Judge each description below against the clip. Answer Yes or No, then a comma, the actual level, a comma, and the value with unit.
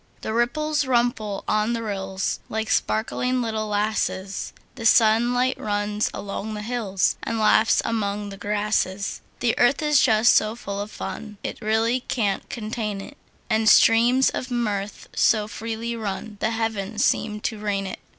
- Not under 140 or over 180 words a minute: Yes, average, 155 wpm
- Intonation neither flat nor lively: No, narrow, 2.2 semitones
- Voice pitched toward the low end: No, high, 220 Hz